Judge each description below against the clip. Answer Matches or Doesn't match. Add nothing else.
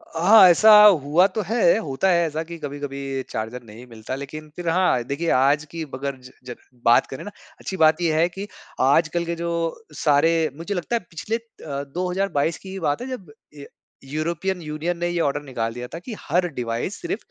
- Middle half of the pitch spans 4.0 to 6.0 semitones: Matches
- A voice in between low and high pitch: Matches